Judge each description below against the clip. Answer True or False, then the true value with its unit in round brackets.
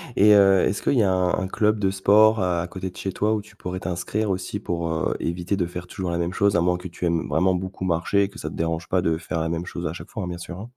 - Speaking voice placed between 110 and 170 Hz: False (90 Hz)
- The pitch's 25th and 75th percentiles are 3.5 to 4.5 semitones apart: False (2.6 semitones)